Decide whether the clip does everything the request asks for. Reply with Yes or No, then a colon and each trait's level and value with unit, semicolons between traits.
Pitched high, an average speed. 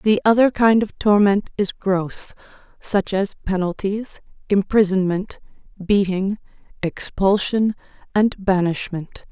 No: high, 200 Hz; slow, 90 wpm